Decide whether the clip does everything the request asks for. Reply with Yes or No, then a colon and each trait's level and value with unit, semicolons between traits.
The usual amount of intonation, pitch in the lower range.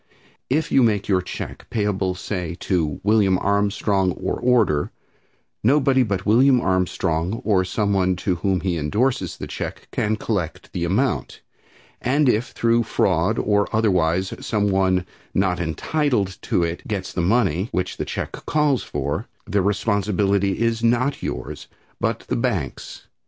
Yes: average, 3.8 semitones; low, 100 Hz